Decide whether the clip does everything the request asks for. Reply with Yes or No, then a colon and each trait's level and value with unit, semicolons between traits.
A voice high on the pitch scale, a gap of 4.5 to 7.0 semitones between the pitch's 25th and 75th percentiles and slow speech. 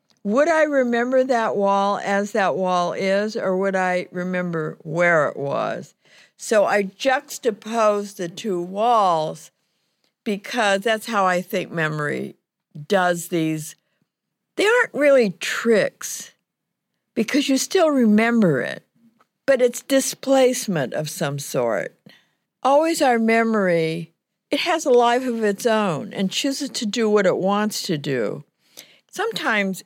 Yes: high, 210 Hz; average, 5.1 semitones; slow, 130 wpm